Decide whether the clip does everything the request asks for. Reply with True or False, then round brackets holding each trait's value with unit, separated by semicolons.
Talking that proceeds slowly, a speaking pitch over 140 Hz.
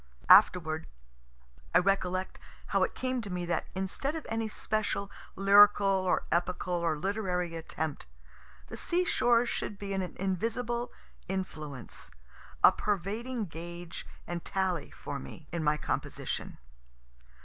True (125 wpm; 190 Hz)